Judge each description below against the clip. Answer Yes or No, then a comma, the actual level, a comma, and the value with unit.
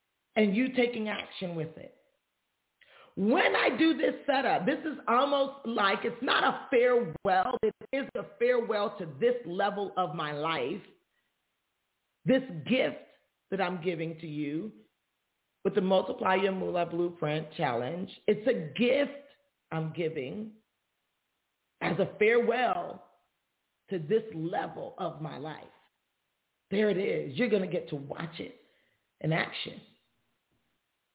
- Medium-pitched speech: No, high, 205 Hz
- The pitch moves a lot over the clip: Yes, wide, 6.4 semitones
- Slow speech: Yes, slow, 130 wpm